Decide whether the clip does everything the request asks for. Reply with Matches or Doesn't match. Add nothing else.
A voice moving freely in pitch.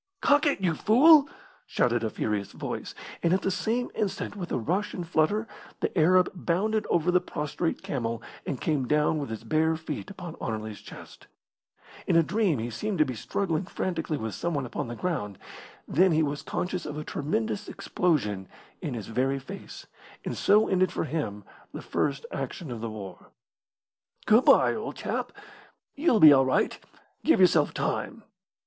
Matches